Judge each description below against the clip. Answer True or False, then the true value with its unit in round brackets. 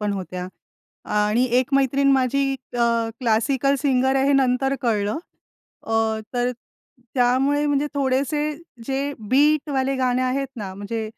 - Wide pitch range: False (2.9 semitones)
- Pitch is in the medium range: False (260 Hz)